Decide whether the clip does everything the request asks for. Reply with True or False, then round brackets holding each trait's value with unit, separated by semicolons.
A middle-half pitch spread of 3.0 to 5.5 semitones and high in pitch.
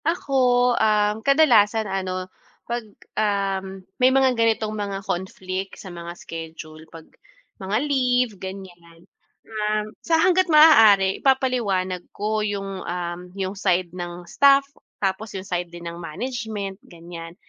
True (4.0 semitones; 195 Hz)